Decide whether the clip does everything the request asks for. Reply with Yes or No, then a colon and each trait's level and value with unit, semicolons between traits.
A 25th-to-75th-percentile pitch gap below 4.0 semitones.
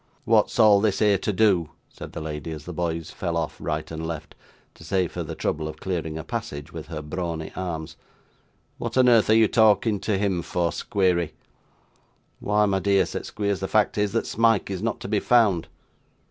No: average, 4.3 semitones